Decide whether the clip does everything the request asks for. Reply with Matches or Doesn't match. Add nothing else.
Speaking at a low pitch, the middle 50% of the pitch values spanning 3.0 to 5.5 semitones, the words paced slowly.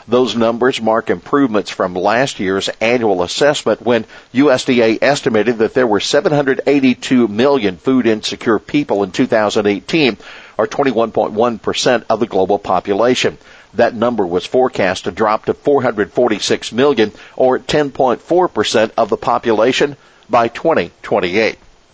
Matches